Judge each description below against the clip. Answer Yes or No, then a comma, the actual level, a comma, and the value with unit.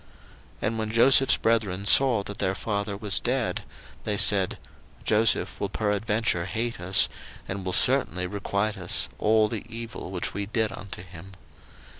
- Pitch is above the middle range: No, low, 105 Hz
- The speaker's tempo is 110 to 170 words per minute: Yes, average, 155 wpm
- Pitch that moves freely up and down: No, average, 2.7 semitones